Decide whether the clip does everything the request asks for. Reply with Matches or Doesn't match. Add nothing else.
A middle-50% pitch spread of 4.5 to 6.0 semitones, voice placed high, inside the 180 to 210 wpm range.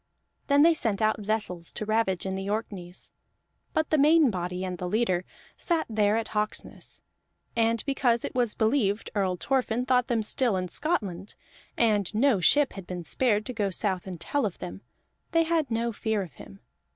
Matches